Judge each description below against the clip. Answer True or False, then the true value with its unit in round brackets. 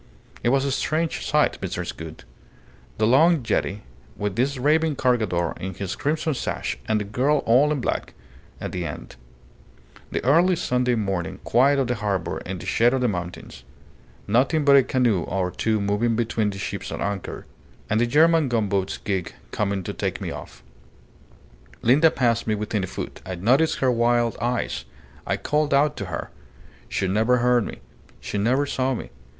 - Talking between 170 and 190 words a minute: True (180 wpm)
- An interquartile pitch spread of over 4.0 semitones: True (5.3 semitones)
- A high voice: False (120 Hz)